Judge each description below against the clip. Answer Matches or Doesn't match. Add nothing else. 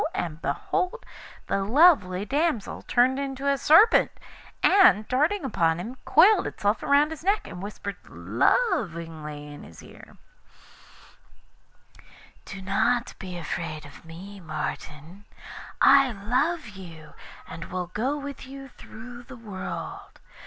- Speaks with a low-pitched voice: Doesn't match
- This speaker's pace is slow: Matches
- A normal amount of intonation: Doesn't match